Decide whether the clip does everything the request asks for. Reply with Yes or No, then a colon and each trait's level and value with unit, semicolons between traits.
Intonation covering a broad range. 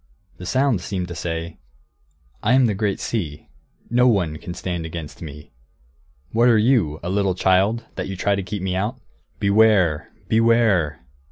No: average, 4.6 semitones